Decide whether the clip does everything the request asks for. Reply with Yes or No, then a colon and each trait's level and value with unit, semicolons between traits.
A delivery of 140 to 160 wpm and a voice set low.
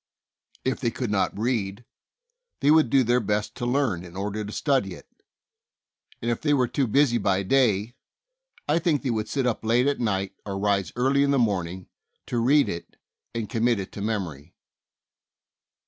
No: average, 180 wpm; low, 115 Hz